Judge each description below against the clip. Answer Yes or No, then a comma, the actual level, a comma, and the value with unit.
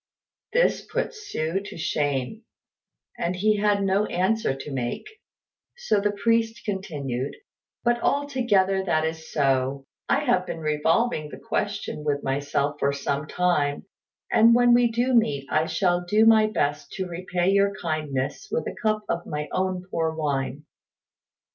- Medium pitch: Yes, medium, 180 Hz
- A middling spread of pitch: No, wide, 6.5 semitones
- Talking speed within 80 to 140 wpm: No, average, 150 wpm